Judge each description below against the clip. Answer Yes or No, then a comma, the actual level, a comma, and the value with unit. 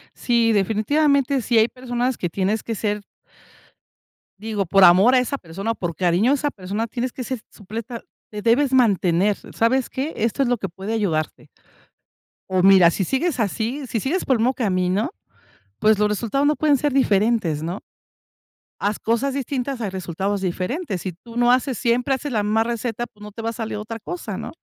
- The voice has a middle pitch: No, high, 225 Hz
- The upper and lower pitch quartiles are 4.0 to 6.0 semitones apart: Yes, average, 4.3 semitones